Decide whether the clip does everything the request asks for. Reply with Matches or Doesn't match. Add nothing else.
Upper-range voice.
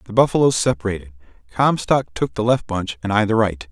Doesn't match